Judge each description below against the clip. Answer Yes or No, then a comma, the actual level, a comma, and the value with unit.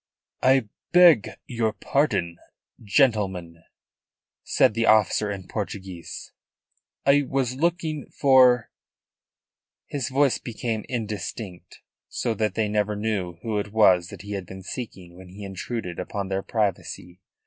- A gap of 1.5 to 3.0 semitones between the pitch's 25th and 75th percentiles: No, average, 4.4 semitones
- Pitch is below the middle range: Yes, low, 105 Hz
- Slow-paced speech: Yes, slow, 130 wpm